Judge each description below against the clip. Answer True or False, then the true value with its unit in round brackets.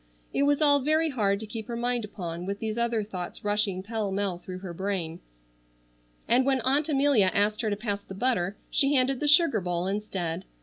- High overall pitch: True (215 Hz)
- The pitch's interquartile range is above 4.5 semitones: True (5.2 semitones)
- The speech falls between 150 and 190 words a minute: False (205 wpm)